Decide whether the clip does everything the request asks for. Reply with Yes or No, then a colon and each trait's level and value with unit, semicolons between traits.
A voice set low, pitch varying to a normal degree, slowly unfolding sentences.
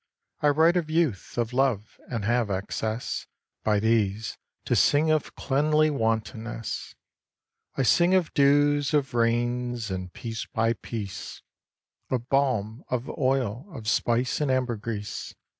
Yes: low, 120 Hz; average, 4.2 semitones; slow, 130 wpm